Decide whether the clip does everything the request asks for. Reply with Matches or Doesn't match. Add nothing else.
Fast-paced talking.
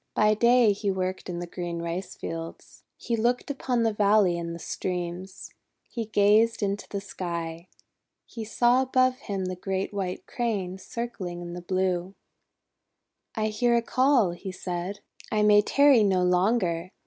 Doesn't match